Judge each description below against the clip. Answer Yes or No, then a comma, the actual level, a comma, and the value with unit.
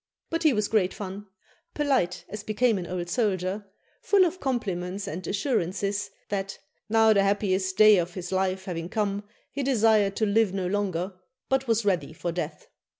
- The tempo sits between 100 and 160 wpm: No, average, 170 wpm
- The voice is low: No, high, 200 Hz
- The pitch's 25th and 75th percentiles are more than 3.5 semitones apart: No, average, 3.1 semitones